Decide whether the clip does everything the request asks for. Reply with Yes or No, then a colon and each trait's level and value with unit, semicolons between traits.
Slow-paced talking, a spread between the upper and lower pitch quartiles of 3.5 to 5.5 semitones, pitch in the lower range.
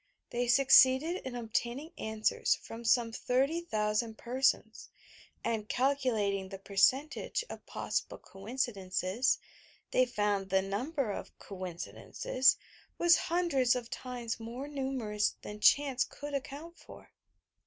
No: slow, 120 wpm; average, 4.5 semitones; high, 240 Hz